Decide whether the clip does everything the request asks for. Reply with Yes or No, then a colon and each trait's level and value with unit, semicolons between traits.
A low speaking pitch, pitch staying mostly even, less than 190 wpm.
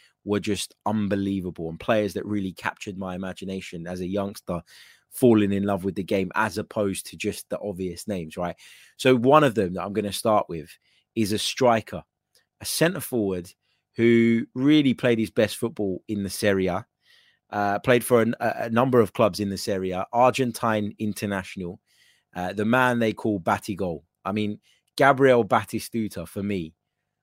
No: low, 105 Hz; average, 3.2 semitones; average, 170 wpm